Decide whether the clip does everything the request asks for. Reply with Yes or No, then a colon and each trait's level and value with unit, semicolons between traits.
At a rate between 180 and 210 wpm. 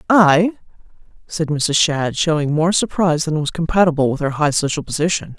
No: average, 165 wpm